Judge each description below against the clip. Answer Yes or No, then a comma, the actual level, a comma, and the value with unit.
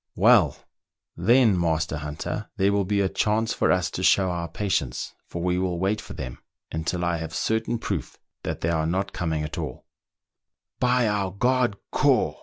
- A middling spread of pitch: Yes, average, 4.1 semitones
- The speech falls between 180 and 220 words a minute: Yes, average, 190 wpm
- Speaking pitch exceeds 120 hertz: No, very low, 95 Hz